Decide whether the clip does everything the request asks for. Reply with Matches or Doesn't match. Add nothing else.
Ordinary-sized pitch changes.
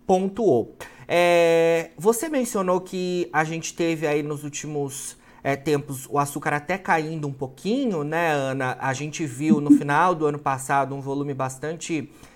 Matches